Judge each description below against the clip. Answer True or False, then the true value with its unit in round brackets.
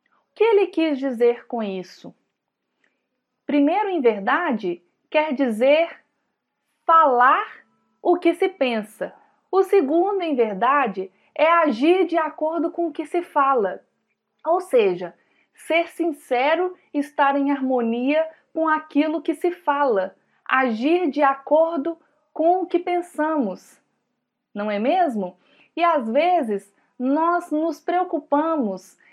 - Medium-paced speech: False (115 wpm)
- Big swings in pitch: False (4.4 semitones)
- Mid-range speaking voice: False (310 Hz)